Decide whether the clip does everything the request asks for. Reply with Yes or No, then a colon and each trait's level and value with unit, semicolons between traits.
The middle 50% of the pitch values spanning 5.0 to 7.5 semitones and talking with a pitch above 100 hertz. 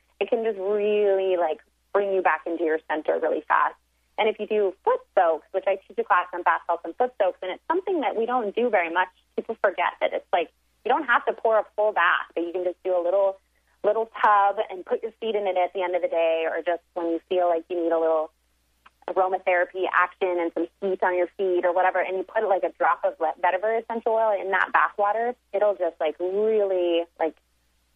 No: average, 3.6 semitones; medium, 185 Hz